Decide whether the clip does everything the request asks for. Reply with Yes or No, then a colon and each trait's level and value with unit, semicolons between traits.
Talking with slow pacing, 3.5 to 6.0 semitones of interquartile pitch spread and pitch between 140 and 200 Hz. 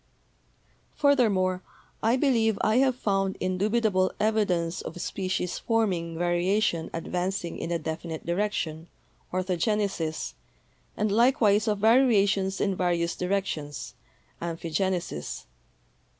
Yes: slow, 105 wpm; average, 3.8 semitones; high, 190 Hz